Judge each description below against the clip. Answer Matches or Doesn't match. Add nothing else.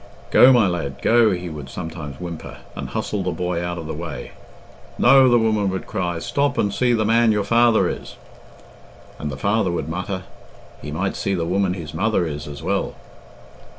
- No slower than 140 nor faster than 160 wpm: Doesn't match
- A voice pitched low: Matches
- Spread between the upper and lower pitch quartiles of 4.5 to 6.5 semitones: Matches